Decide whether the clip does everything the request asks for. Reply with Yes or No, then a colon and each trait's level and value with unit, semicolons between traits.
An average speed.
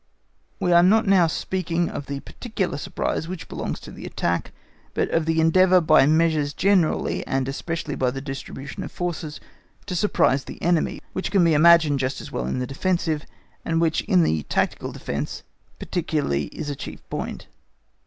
Yes: average, 175 wpm